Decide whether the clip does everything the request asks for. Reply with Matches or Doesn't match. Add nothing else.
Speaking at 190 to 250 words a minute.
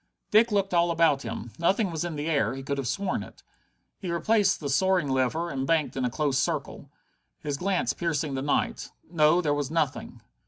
Matches